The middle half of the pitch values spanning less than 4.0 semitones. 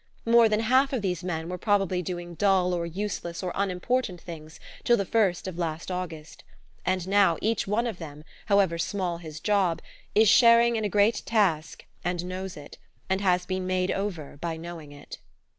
Yes: average, 3.4 semitones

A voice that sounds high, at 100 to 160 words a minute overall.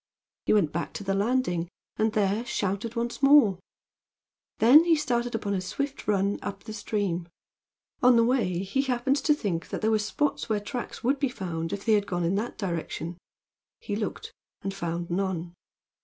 No: high, 205 Hz; average, 185 wpm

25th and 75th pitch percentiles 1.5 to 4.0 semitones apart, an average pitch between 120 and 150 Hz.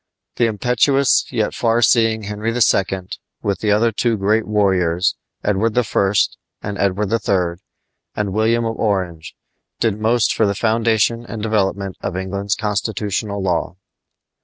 No: narrow, 2.5 semitones; low, 105 Hz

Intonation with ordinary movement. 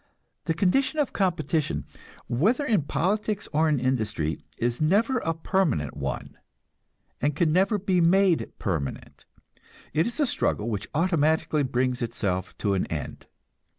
No: wide, 8.1 semitones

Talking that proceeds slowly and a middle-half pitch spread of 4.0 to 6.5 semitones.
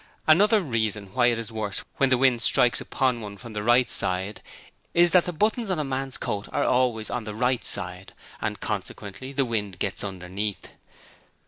No: average, 190 wpm; average, 4.4 semitones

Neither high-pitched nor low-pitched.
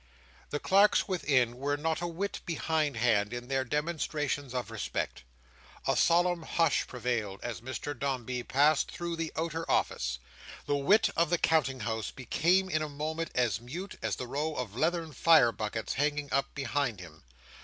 Yes: medium, 145 Hz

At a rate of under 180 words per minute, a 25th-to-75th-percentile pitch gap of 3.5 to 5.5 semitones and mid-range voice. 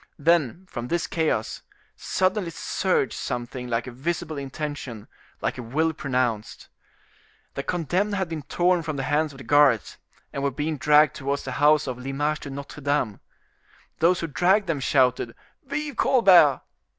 Yes: average, 160 wpm; average, 4.4 semitones; medium, 145 Hz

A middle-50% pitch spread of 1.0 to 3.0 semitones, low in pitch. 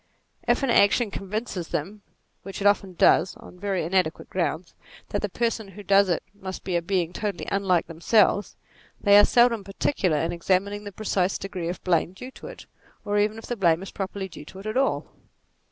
No: narrow, 2.4 semitones; high, 195 Hz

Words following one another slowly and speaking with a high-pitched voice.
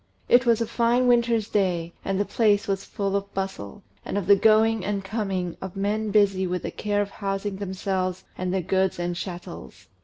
No: average, 195 wpm; high, 195 Hz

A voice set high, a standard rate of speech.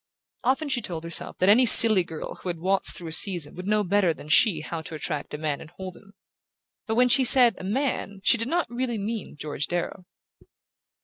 No: high, 195 Hz; fast, 220 wpm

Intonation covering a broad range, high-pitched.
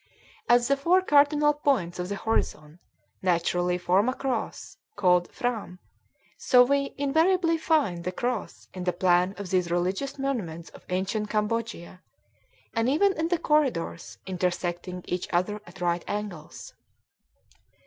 Yes: wide, 7.6 semitones; high, 205 Hz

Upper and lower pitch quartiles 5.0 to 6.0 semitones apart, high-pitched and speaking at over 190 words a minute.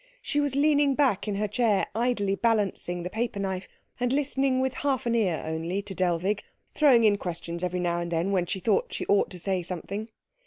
Yes: wide, 5.5 semitones; high, 205 Hz; fast, 205 wpm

